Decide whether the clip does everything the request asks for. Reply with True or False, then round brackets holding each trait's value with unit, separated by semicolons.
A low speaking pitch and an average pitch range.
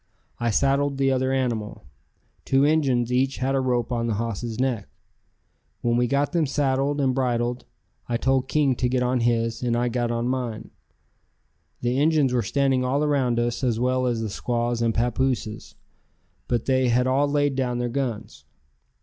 False (125 Hz; 2.2 semitones)